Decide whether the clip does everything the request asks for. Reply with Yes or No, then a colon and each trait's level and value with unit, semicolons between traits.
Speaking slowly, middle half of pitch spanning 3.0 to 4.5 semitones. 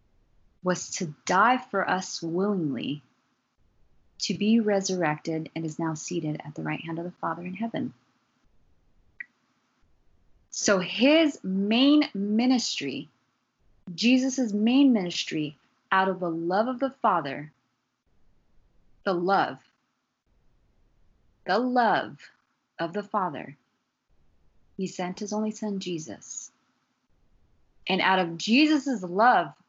No: slow, 110 wpm; wide, 5.4 semitones